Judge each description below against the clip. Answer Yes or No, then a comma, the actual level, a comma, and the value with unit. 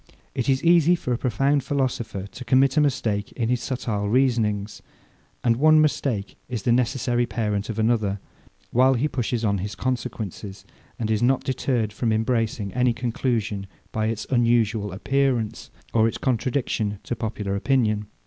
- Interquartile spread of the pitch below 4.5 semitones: Yes, average, 3.4 semitones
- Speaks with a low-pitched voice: Yes, low, 120 Hz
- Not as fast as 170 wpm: Yes, average, 160 wpm